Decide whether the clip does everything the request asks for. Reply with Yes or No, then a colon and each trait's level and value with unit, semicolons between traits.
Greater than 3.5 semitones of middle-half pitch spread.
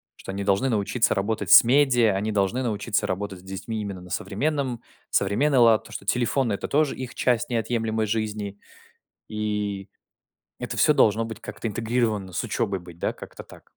No: average, 3.2 semitones